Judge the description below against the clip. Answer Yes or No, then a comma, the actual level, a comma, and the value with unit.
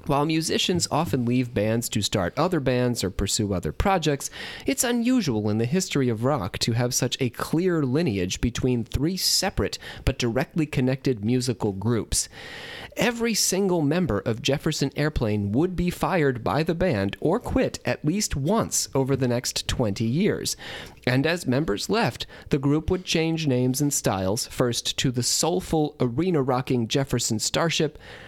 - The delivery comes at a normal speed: Yes, average, 160 wpm